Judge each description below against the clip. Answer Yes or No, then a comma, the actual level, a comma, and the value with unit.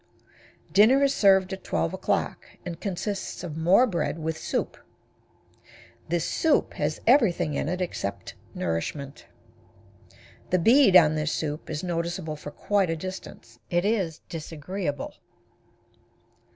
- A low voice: No, medium, 175 Hz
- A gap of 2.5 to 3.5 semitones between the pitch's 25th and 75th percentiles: No, average, 4.0 semitones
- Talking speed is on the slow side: Yes, slow, 125 wpm